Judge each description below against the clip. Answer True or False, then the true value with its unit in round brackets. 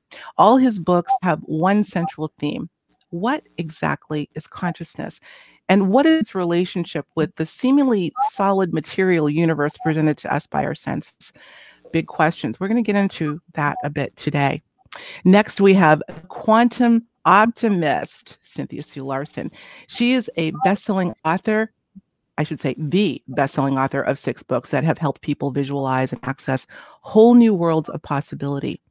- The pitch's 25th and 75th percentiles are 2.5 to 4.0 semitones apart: False (5.2 semitones)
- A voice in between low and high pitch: True (165 Hz)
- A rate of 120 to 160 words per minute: True (145 wpm)